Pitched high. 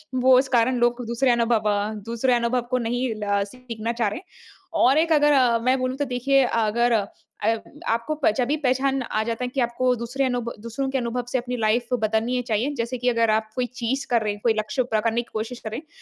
Yes: high, 240 Hz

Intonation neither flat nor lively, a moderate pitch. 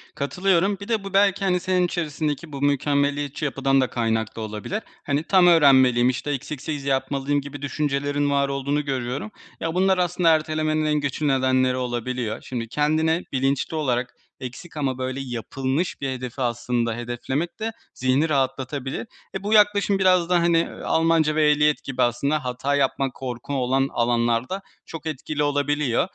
Yes: average, 3.8 semitones; medium, 145 Hz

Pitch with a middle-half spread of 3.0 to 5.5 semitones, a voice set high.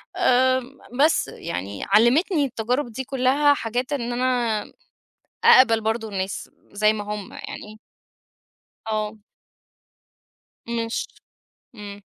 Yes: average, 3.4 semitones; high, 235 Hz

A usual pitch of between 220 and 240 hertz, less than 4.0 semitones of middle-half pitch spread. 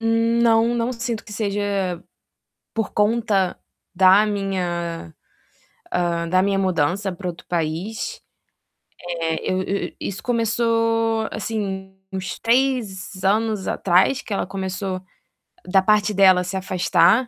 No: high, 195 Hz; average, 3.3 semitones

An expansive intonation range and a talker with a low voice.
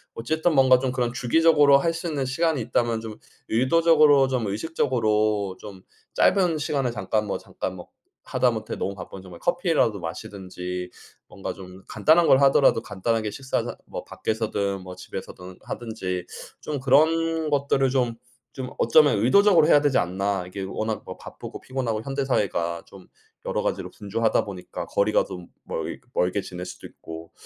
Yes: wide, 6.4 semitones; low, 115 Hz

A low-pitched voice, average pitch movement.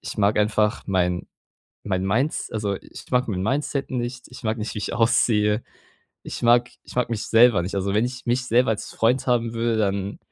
Yes: low, 115 Hz; average, 3.0 semitones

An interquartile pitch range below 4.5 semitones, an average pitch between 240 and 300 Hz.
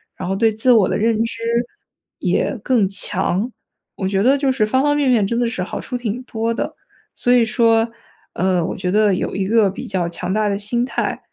No: average, 3.7 semitones; high, 220 Hz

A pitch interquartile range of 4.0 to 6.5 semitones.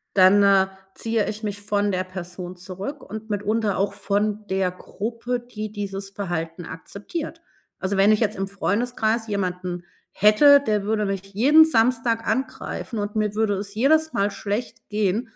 No: narrow, 2.6 semitones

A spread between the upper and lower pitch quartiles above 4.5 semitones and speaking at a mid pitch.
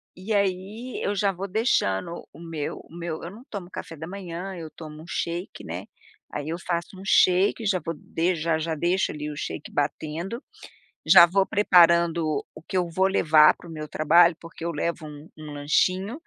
No: average, 3.3 semitones; medium, 170 Hz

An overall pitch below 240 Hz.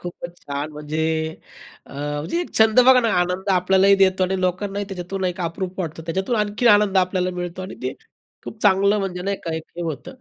Yes: medium, 185 Hz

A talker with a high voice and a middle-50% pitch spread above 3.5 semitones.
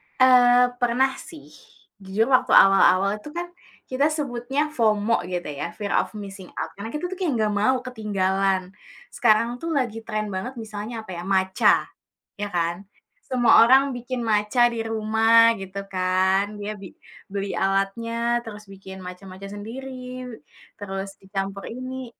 Yes: high, 215 Hz; average, 3.9 semitones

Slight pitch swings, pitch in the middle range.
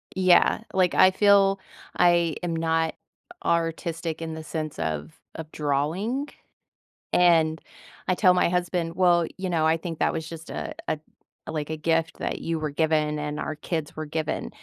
Yes: narrow, 2.0 semitones; medium, 165 Hz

